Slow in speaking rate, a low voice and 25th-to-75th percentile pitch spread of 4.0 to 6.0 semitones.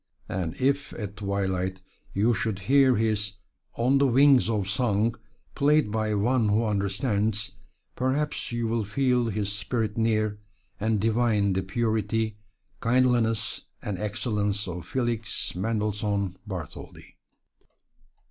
No: slow, 120 wpm; low, 110 Hz; average, 2.8 semitones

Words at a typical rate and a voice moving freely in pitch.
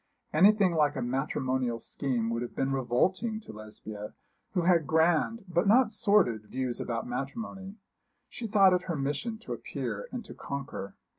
Yes: average, 160 wpm; wide, 7.9 semitones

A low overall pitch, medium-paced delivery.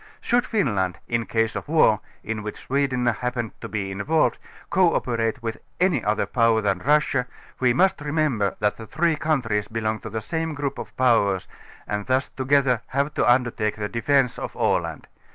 Yes: low, 120 Hz; average, 180 wpm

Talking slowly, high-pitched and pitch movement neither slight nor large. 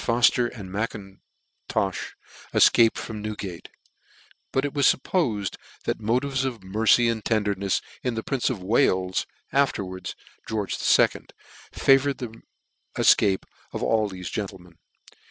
No: slow, 125 wpm; low, 110 Hz; average, 4.1 semitones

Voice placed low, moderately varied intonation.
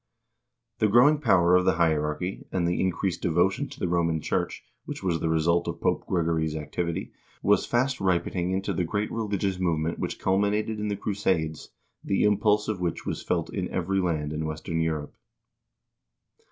Yes: very low, 90 Hz; average, 3.8 semitones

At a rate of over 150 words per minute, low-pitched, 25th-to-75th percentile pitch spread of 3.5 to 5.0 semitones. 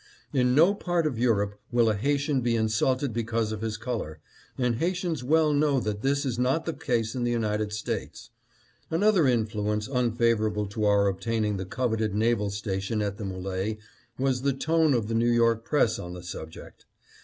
Yes: average, 185 wpm; low, 115 Hz; average, 4.0 semitones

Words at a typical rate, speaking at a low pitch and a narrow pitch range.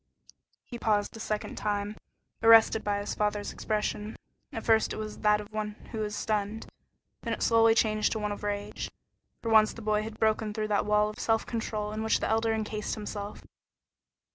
No: average, 190 wpm; high, 215 Hz; narrow, 1.0 semitones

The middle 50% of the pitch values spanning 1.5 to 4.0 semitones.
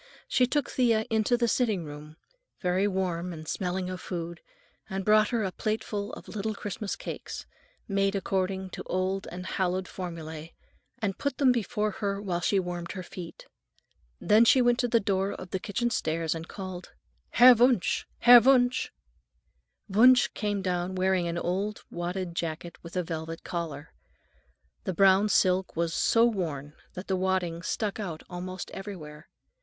Yes: average, 3.4 semitones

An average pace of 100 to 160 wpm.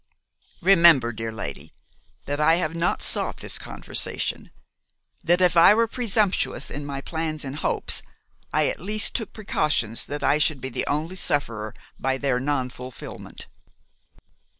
Yes: average, 145 wpm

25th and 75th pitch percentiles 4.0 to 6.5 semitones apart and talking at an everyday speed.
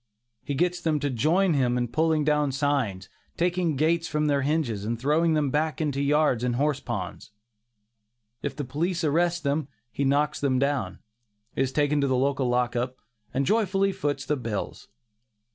No: average, 3.4 semitones; average, 170 wpm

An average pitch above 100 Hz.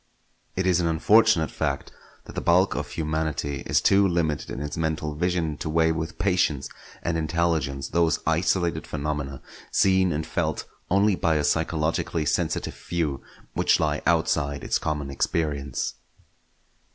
No: very low, 80 Hz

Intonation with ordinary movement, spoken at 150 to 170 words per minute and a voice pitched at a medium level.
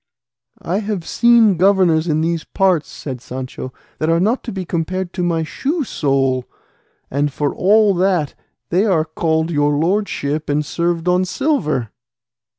Yes: average, 4.2 semitones; average, 155 wpm; medium, 170 Hz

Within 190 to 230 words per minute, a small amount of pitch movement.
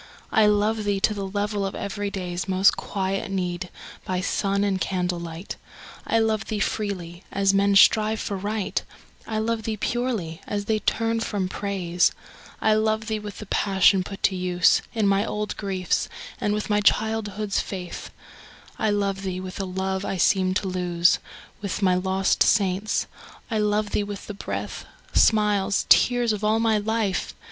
No: average, 170 wpm; narrow, 2.2 semitones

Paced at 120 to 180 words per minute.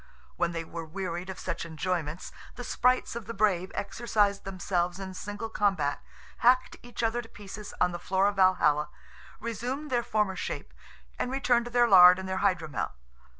Yes: average, 175 wpm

